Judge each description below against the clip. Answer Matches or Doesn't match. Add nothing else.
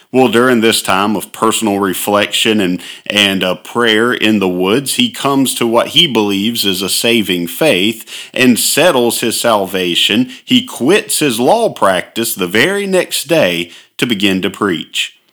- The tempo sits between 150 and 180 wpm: Matches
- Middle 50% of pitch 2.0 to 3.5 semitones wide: Doesn't match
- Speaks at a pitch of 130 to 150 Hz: Doesn't match